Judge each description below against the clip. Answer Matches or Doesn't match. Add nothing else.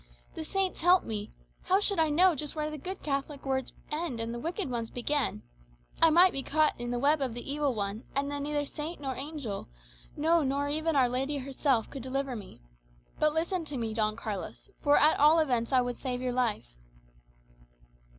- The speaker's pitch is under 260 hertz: Doesn't match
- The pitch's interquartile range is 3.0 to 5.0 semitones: Matches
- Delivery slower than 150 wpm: Doesn't match